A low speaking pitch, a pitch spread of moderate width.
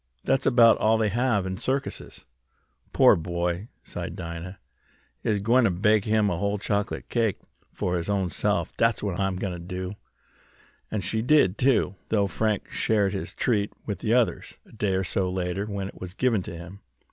Yes: low, 100 Hz; average, 3.1 semitones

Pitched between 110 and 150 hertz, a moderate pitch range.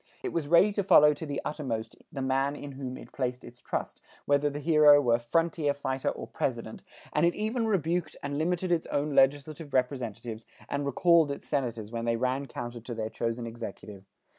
Yes: medium, 140 Hz; average, 4.1 semitones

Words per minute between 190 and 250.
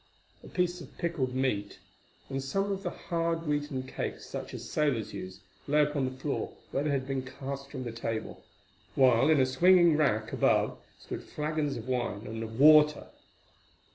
No: average, 175 wpm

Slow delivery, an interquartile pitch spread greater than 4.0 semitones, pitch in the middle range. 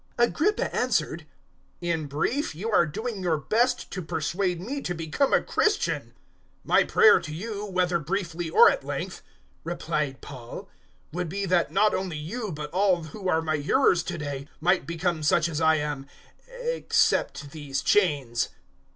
No: average, 165 wpm; average, 4.6 semitones; medium, 170 Hz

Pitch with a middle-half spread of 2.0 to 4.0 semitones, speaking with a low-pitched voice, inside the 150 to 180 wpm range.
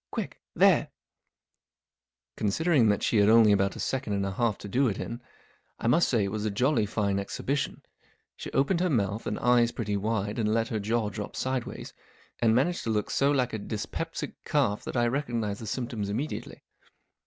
No: average, 3.3 semitones; low, 115 Hz; average, 195 wpm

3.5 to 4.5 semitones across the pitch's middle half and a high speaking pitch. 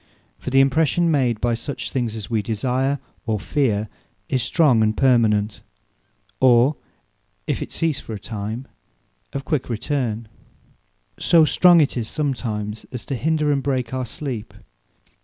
No: average, 4.2 semitones; low, 125 Hz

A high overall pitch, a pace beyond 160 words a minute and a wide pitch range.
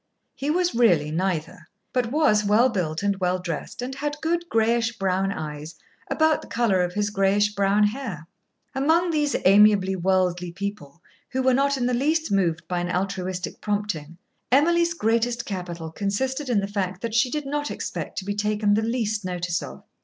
Yes: high, 205 Hz; average, 180 wpm; wide, 5.7 semitones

